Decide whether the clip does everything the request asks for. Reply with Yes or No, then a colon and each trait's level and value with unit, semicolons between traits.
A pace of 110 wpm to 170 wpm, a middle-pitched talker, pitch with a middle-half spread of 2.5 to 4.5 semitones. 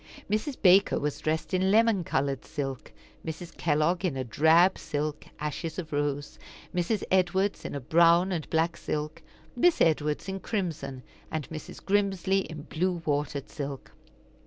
Yes: average, 150 wpm; medium, 165 Hz; average, 4.2 semitones